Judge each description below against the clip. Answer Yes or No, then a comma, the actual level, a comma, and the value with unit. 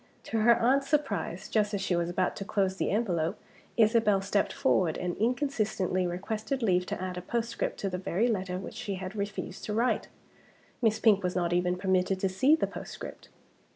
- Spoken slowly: No, average, 190 wpm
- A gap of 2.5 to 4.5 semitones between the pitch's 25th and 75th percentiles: Yes, average, 3.6 semitones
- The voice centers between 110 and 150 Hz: No, high, 200 Hz